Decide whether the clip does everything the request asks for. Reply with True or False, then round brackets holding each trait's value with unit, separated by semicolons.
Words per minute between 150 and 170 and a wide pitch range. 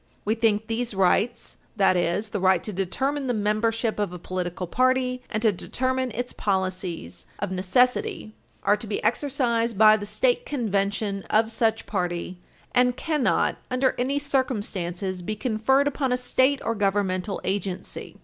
False (155 wpm; 4.5 semitones)